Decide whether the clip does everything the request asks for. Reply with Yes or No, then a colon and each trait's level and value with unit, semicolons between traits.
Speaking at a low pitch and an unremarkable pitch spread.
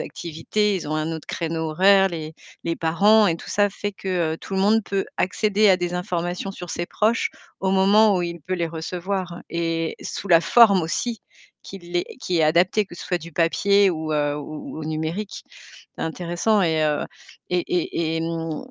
No: medium, 175 Hz; average, 3.1 semitones